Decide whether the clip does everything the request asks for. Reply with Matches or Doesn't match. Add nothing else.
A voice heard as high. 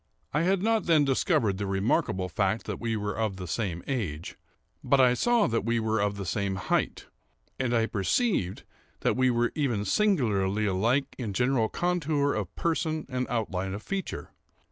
Doesn't match